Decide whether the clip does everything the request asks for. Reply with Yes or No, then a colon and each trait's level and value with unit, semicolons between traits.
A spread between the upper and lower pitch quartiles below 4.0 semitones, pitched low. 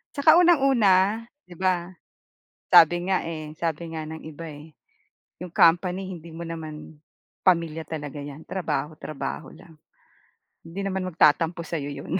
No: average, 3.0 semitones; medium, 165 Hz